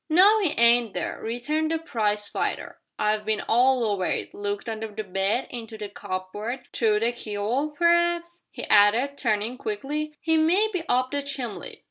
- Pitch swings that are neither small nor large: No, wide, 6.3 semitones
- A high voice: Yes, high, 240 Hz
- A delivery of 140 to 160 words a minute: No, average, 170 wpm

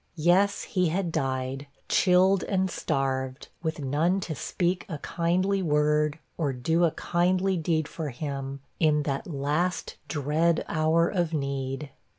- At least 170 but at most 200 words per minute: No, average, 145 wpm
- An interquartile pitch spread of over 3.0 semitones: Yes, average, 4.0 semitones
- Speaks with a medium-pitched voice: Yes, medium, 160 Hz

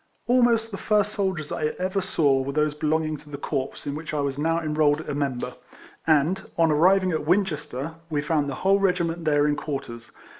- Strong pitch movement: No, average, 4.1 semitones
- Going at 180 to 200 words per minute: Yes, average, 195 wpm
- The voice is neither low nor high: Yes, medium, 155 Hz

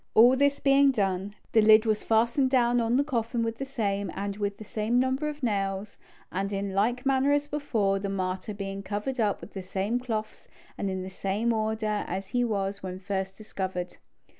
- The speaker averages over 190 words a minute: Yes, average, 200 wpm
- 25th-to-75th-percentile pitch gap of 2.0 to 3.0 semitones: No, average, 3.8 semitones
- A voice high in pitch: Yes, high, 215 Hz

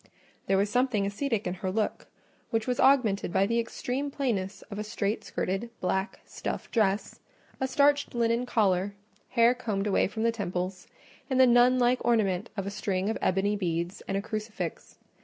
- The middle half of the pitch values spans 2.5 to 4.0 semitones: Yes, average, 3.7 semitones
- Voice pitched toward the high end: Yes, high, 215 Hz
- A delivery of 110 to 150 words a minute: No, average, 175 wpm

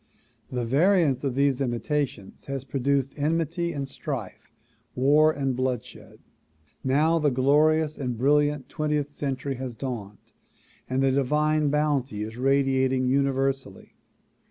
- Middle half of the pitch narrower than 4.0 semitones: Yes, narrow, 2.4 semitones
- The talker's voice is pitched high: No, low, 135 Hz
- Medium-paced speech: No, slow, 125 wpm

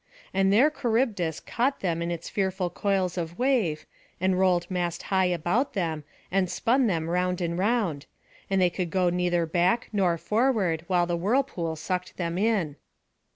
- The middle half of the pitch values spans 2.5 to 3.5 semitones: Yes, average, 3.0 semitones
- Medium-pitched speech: Yes, medium, 180 Hz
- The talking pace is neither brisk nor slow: Yes, average, 165 wpm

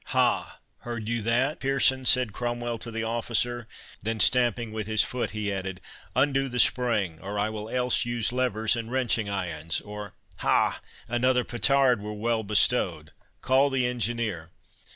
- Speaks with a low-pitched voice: Yes, low, 115 Hz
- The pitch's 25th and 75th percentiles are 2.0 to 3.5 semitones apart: Yes, average, 2.9 semitones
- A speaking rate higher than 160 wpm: No, average, 150 wpm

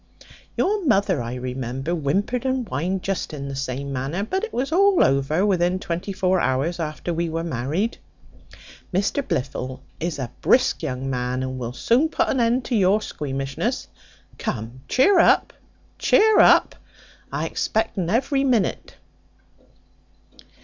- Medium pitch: Yes, medium, 175 Hz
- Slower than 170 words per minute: Yes, average, 150 wpm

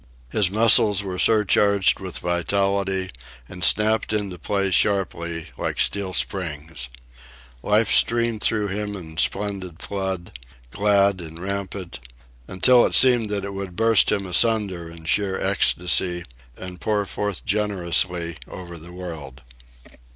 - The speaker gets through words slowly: Yes, slow, 130 wpm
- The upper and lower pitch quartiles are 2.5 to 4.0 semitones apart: Yes, average, 2.8 semitones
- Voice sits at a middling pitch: No, very low, 95 Hz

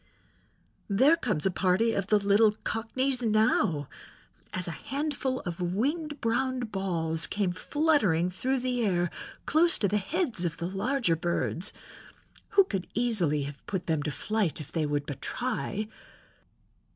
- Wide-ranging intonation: Yes, wide, 6.6 semitones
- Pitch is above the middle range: Yes, high, 205 Hz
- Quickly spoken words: No, average, 150 wpm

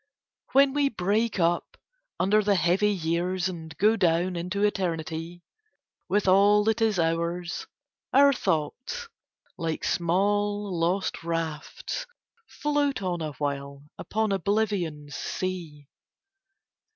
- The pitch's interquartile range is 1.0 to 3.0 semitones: No, average, 3.9 semitones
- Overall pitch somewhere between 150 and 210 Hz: Yes, medium, 185 Hz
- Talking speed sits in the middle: No, slow, 105 wpm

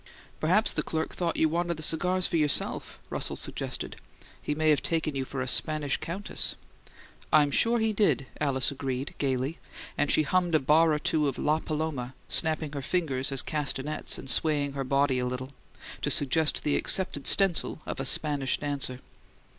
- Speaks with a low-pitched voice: No, medium, 150 Hz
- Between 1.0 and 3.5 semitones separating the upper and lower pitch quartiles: Yes, average, 2.9 semitones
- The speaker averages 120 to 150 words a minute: No, average, 175 wpm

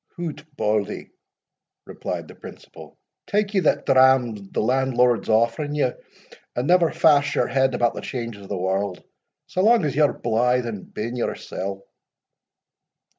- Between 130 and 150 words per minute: Yes, average, 145 wpm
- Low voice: Yes, low, 125 Hz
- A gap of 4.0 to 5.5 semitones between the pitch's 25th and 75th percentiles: Yes, average, 5.0 semitones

